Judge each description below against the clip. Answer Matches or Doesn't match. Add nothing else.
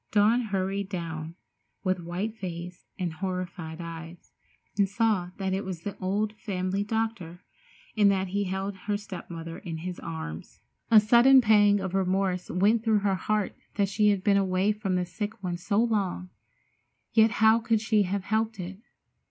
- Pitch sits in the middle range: Doesn't match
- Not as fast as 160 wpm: Doesn't match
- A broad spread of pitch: Doesn't match